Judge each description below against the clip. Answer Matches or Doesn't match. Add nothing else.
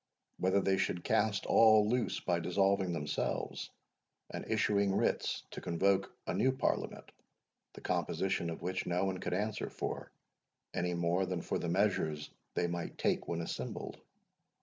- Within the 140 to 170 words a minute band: Matches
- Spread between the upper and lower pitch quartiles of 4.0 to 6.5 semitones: Doesn't match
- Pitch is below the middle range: Matches